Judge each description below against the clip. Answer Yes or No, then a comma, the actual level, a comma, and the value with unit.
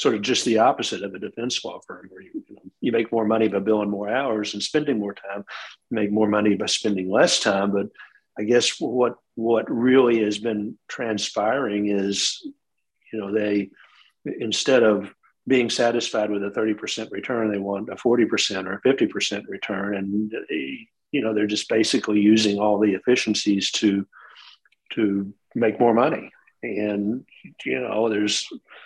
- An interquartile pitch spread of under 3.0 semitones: Yes, narrow, 2.4 semitones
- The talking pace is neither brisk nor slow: Yes, average, 170 wpm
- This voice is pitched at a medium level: No, low, 105 Hz